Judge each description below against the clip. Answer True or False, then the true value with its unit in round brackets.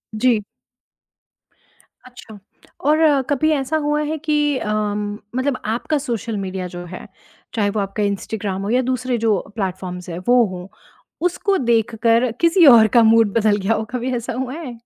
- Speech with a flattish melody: False (4.3 semitones)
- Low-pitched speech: False (230 Hz)